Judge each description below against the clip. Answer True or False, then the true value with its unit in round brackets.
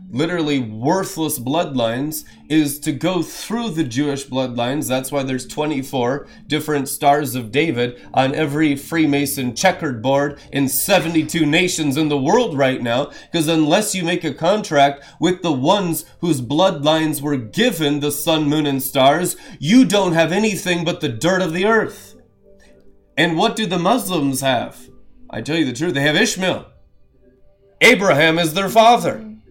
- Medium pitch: True (155 Hz)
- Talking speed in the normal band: True (155 wpm)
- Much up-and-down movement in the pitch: False (4.0 semitones)